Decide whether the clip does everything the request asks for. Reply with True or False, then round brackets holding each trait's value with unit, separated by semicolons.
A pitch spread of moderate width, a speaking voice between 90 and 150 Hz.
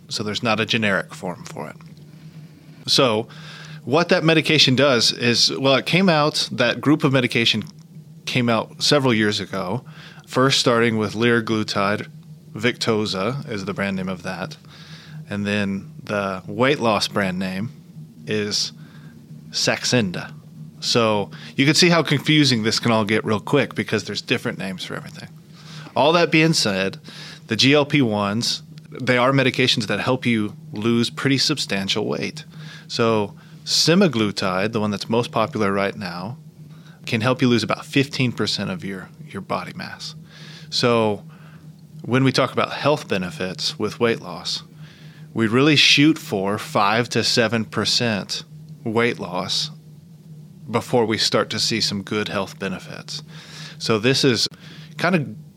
False (6.0 semitones; 140 Hz)